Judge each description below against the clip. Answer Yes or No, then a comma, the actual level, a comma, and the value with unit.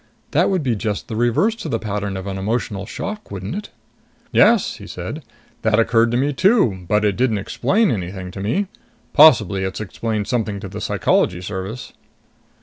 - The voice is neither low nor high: No, low, 110 Hz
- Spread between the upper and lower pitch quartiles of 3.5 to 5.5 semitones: Yes, average, 4.2 semitones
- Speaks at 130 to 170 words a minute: No, average, 180 wpm